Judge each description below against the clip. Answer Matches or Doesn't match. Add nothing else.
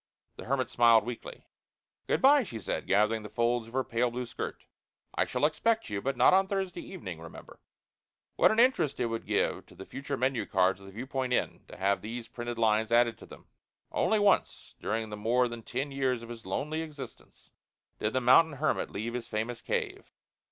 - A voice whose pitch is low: Matches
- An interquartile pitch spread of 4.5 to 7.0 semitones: Doesn't match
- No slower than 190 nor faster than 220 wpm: Matches